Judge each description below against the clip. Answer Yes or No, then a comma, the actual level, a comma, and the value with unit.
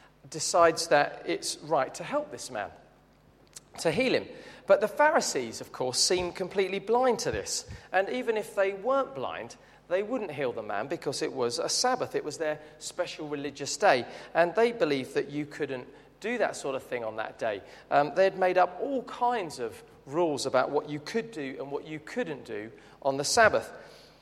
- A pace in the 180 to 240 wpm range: Yes, average, 195 wpm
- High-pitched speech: Yes, high, 195 Hz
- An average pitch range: No, wide, 9.0 semitones